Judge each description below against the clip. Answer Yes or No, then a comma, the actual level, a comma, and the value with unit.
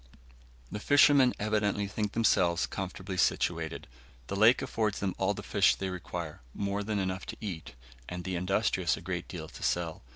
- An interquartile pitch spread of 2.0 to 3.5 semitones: Yes, average, 2.7 semitones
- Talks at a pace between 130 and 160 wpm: No, average, 170 wpm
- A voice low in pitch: Yes, very low, 95 Hz